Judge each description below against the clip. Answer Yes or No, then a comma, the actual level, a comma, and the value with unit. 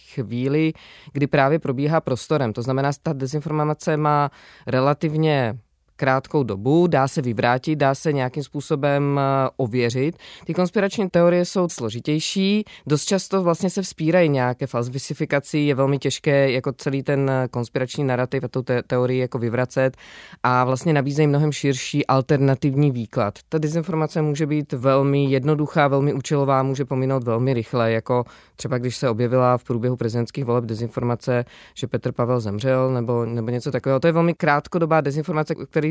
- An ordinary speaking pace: Yes, average, 150 wpm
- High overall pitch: No, medium, 140 Hz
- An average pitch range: Yes, average, 3.3 semitones